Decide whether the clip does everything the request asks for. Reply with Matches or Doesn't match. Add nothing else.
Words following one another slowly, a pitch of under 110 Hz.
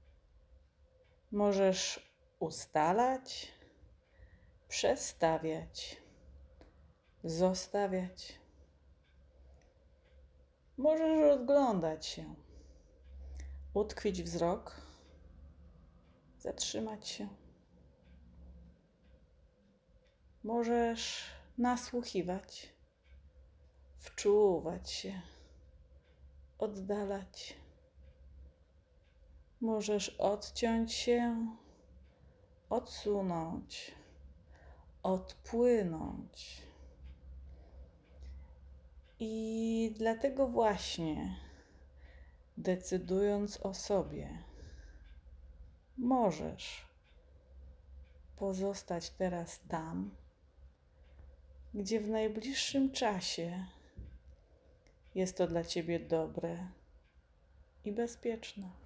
Matches